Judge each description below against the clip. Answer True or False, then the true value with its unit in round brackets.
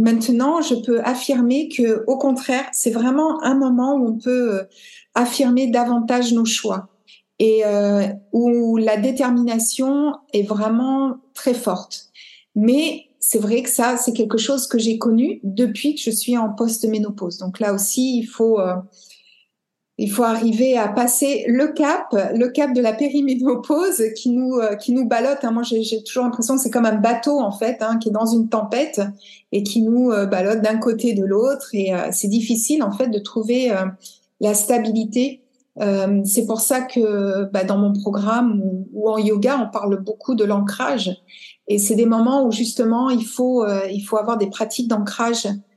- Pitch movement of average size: True (3.1 semitones)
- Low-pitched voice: False (230 Hz)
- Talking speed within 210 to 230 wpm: False (180 wpm)